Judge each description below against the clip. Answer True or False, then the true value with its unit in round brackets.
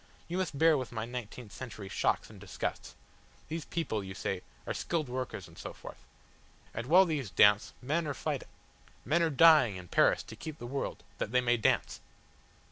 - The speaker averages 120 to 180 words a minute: False (190 wpm)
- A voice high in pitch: False (130 Hz)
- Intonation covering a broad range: True (6.3 semitones)